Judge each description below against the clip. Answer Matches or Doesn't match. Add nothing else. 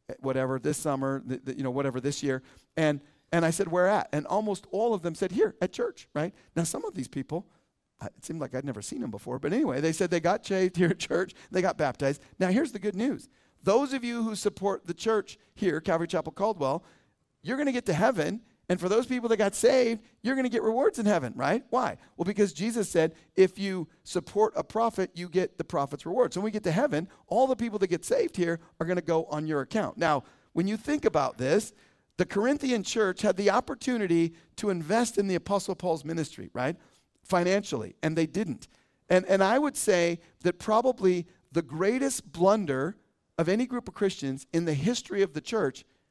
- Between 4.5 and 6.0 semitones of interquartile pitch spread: Matches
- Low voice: Doesn't match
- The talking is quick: Matches